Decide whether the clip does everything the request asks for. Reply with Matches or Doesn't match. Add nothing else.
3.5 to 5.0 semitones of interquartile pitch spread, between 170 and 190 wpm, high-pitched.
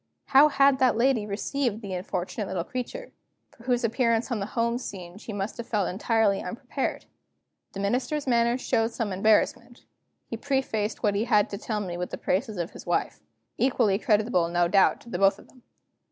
Matches